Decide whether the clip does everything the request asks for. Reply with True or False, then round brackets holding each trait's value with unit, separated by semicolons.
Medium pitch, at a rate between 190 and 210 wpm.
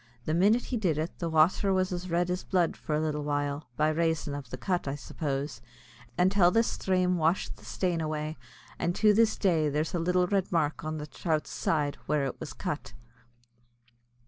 True (165 Hz; 195 wpm)